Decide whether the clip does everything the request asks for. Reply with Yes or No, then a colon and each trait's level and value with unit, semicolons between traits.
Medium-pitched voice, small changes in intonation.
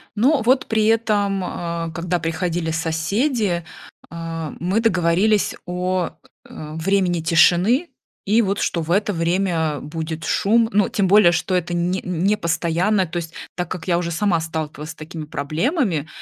No: medium, 175 Hz; average, 3.7 semitones